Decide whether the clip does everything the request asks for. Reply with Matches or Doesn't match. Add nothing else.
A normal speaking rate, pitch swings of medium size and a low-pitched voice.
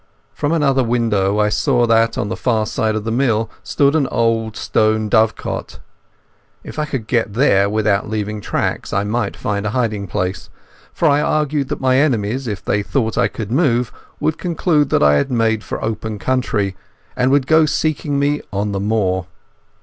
Matches